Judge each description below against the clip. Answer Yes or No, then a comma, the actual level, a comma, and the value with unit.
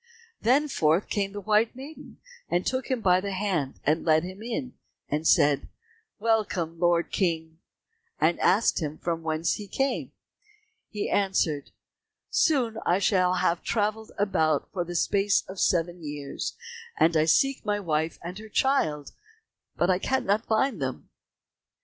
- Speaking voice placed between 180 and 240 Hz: Yes, medium, 185 Hz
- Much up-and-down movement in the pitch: No, average, 5.0 semitones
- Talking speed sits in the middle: Yes, average, 145 wpm